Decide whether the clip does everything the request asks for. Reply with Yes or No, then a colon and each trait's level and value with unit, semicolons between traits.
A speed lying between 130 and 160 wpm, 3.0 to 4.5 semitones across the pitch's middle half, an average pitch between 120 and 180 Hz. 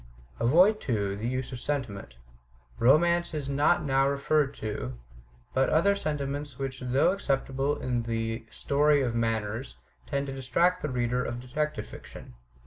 Yes: average, 145 wpm; average, 3.8 semitones; low, 135 Hz